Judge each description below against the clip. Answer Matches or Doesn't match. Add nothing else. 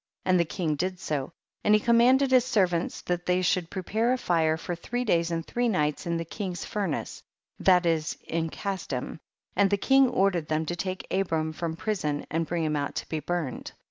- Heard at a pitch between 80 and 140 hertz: Doesn't match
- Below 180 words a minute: Doesn't match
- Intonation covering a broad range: Doesn't match